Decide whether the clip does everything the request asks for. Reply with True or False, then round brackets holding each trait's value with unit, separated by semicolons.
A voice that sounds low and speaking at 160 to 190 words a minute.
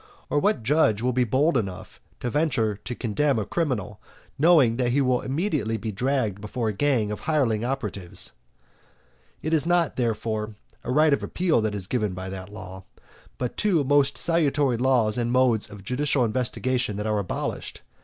True (125 Hz; 175 wpm)